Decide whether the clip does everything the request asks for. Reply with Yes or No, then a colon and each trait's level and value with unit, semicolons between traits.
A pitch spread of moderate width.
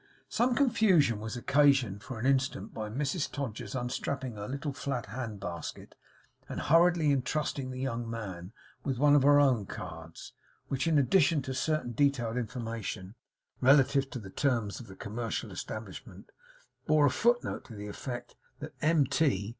Yes: average, 4.2 semitones